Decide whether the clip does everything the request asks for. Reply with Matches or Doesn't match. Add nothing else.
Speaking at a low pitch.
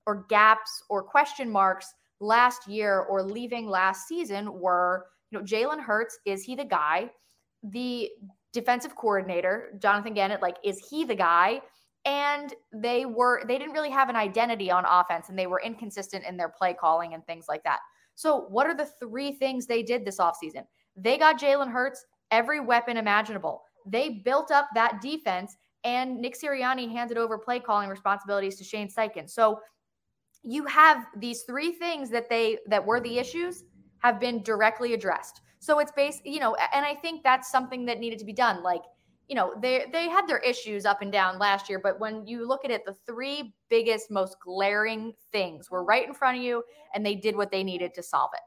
Doesn't match